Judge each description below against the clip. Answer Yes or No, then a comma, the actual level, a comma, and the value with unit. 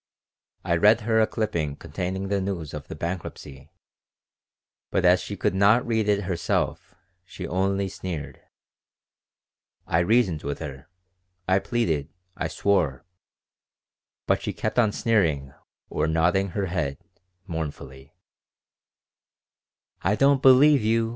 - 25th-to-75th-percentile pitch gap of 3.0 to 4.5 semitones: No, average, 5.3 semitones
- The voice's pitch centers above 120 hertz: No, very low, 95 Hz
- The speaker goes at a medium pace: No, slow, 120 wpm